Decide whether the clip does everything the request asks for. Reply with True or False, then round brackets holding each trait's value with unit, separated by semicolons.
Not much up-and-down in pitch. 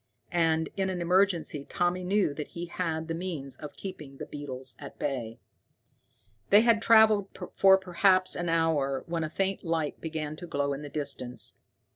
False (4.2 semitones)